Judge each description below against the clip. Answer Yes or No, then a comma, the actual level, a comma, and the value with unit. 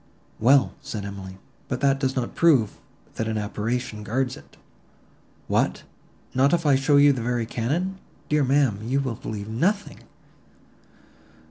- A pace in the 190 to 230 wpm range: No, average, 145 wpm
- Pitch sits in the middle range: No, low, 130 Hz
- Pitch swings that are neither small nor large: Yes, average, 4.1 semitones